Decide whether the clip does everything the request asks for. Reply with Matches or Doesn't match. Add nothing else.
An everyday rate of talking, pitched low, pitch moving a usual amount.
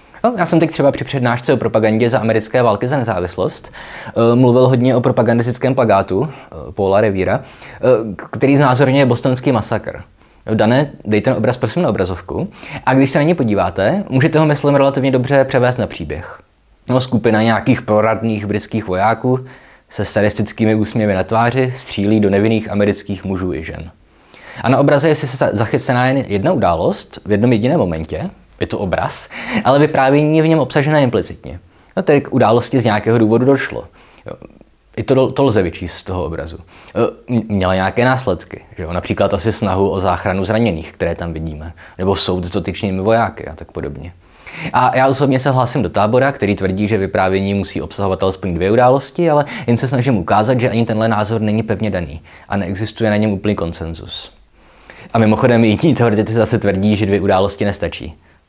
Doesn't match